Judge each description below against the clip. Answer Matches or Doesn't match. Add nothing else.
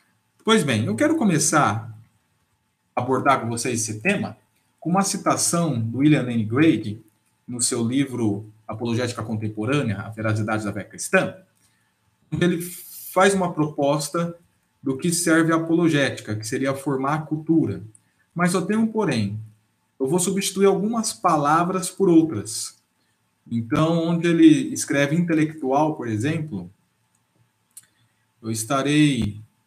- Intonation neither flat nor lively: Doesn't match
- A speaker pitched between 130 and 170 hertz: Matches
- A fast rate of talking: Doesn't match